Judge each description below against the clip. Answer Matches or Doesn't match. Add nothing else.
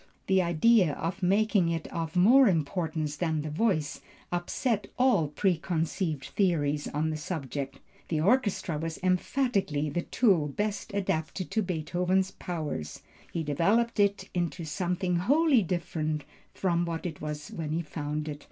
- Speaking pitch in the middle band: Matches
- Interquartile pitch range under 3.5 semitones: Doesn't match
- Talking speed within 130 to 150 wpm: Matches